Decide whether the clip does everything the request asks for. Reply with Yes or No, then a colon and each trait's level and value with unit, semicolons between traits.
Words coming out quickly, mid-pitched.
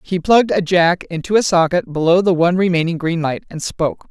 Yes: fast, 220 wpm; medium, 175 Hz